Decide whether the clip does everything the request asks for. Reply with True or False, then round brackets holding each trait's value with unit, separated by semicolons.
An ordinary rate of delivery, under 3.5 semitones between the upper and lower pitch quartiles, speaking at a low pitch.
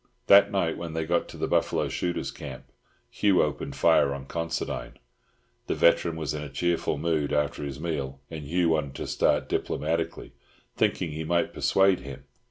True (175 wpm; 2.8 semitones; 80 Hz)